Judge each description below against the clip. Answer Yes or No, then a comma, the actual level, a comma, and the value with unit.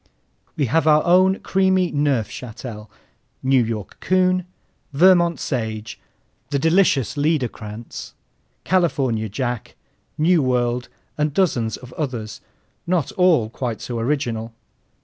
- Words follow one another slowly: Yes, slow, 105 wpm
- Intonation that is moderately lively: No, wide, 6.7 semitones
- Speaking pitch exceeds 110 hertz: Yes, low, 135 Hz